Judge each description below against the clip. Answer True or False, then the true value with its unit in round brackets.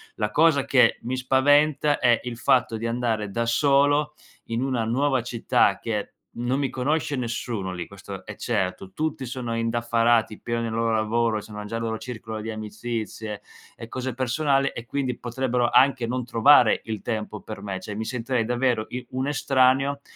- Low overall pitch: True (120 Hz)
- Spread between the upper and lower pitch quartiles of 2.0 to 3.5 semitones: True (2.9 semitones)